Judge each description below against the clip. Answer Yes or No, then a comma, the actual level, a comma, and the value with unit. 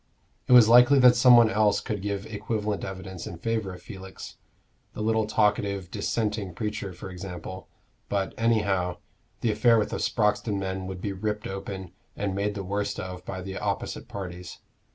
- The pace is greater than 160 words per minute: Yes, average, 175 wpm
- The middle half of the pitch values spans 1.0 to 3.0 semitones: Yes, narrow, 2.4 semitones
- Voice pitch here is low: Yes, low, 100 Hz